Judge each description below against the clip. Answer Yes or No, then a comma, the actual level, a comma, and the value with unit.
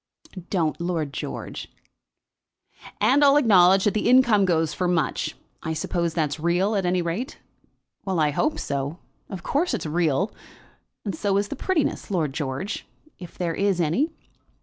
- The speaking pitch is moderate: Yes, medium, 180 Hz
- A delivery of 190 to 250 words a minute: No, average, 155 wpm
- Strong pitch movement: No, average, 4.3 semitones